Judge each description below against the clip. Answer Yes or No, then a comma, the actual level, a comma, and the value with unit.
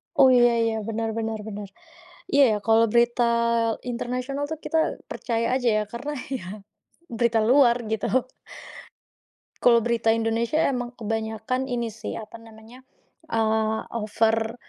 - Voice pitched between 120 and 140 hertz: No, high, 230 Hz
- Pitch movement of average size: No, narrow, 2.0 semitones